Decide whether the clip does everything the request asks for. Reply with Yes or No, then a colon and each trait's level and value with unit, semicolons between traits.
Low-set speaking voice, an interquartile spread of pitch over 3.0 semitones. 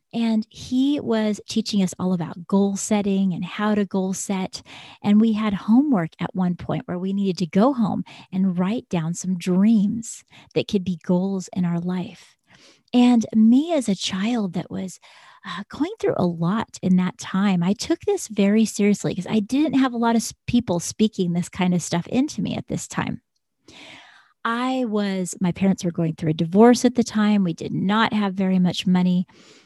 No: high, 200 Hz; average, 3.5 semitones